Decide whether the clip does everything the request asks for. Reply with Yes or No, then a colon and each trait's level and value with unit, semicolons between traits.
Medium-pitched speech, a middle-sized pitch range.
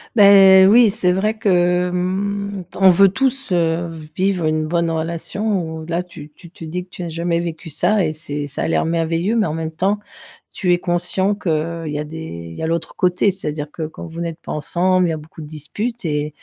Yes: medium, 175 Hz; average, 3.0 semitones